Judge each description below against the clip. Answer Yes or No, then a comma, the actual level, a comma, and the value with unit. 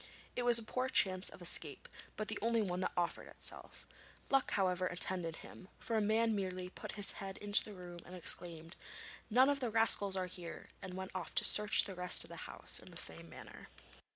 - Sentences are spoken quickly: Yes, fast, 210 wpm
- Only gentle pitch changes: No, average, 3.2 semitones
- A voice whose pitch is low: No, high, 190 Hz